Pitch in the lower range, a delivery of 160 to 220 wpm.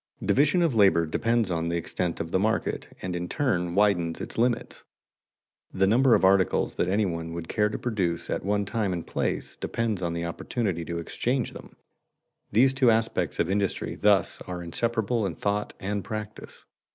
Yes: low, 100 Hz; average, 180 wpm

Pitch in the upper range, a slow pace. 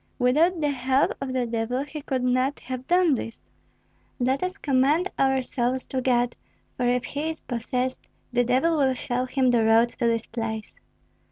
No: very high, 255 Hz; average, 180 wpm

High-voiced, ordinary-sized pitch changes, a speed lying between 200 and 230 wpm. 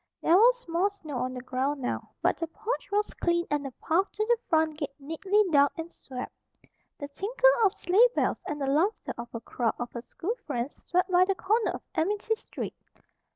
No: very high, 330 Hz; wide, 6.3 semitones; fast, 205 wpm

